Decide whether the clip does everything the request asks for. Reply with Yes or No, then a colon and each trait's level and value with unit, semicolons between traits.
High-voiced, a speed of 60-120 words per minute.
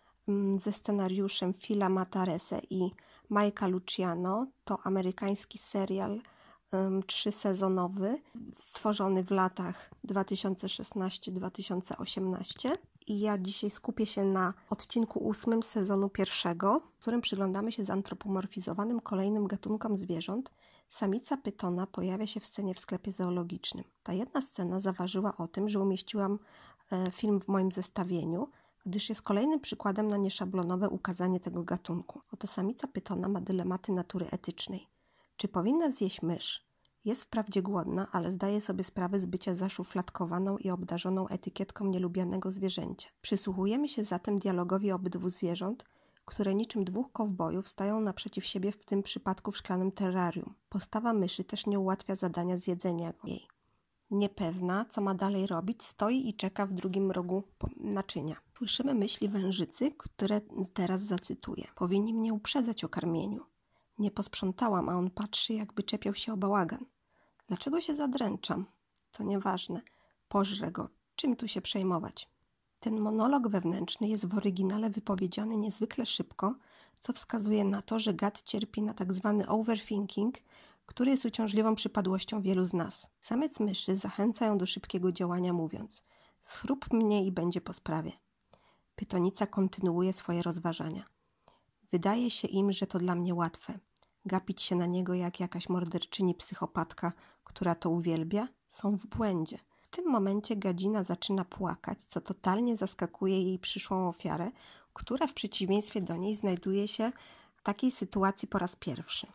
No: high, 195 Hz; average, 140 wpm